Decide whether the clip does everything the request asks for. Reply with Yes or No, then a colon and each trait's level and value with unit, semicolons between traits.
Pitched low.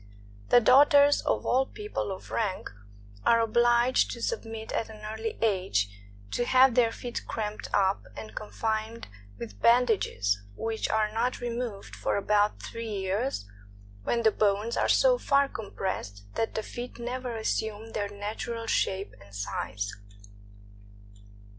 No: high, 220 Hz